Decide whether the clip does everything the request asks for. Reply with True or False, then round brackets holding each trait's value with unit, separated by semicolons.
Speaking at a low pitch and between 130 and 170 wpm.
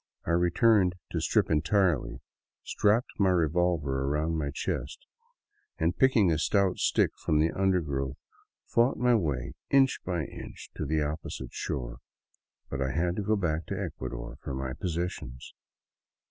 True (80 Hz; 150 wpm)